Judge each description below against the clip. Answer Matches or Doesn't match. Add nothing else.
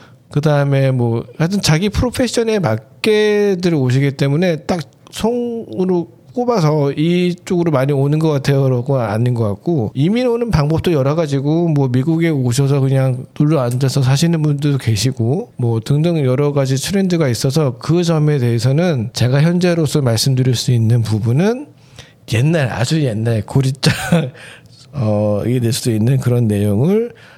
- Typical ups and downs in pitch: Matches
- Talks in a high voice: Doesn't match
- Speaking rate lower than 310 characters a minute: Doesn't match